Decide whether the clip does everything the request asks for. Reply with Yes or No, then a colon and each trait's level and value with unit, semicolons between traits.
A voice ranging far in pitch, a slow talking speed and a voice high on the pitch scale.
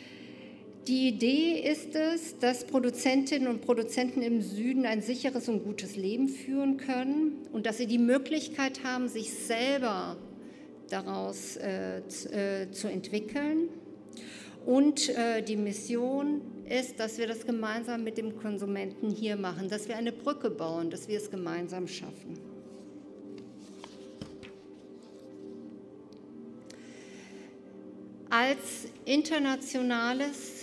Yes: wide, 6.3 semitones; slow, 110 wpm; high, 230 Hz